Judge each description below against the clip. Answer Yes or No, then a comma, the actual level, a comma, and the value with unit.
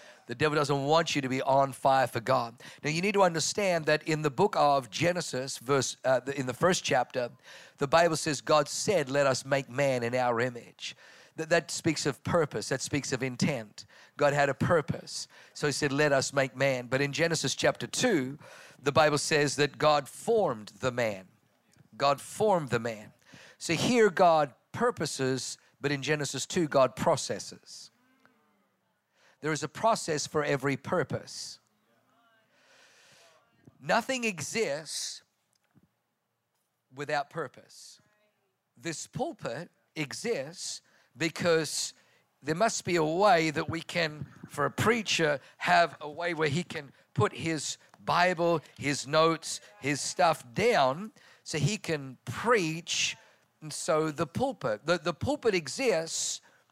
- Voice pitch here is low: No, medium, 150 Hz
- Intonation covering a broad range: No, average, 3.7 semitones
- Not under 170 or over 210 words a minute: No, average, 145 wpm